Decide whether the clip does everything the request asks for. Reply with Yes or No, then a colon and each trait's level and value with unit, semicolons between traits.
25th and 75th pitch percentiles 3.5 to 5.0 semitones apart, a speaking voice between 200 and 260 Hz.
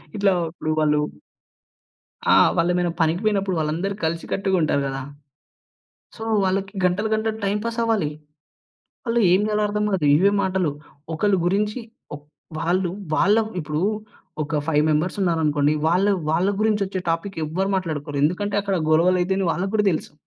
No: average, 3.9 semitones; medium, 185 Hz